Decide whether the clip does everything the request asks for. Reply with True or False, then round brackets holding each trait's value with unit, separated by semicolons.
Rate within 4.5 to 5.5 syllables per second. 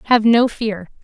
False (4.1 syllables/s)